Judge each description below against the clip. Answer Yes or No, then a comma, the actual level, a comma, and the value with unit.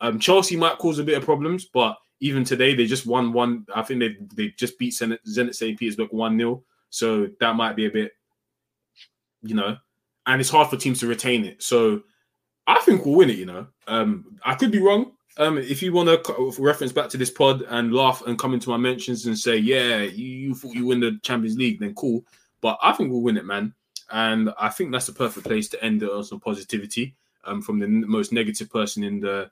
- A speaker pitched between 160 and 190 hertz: No, low, 125 Hz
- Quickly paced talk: Yes, fast, 235 wpm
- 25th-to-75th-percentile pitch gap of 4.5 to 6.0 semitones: Yes, average, 5.2 semitones